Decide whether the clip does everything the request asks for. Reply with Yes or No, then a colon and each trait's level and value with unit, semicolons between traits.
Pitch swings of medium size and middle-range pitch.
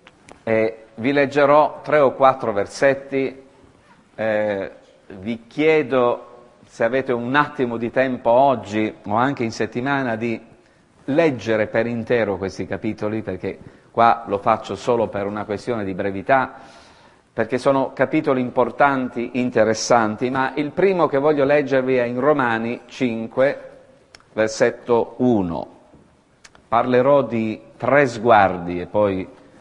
No: average, 3.5 semitones; low, 120 Hz